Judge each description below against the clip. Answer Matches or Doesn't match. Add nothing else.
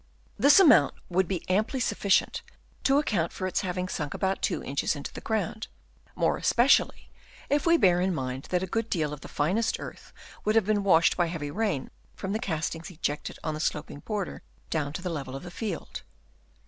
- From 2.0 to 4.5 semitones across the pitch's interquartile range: Doesn't match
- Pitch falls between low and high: Matches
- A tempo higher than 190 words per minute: Matches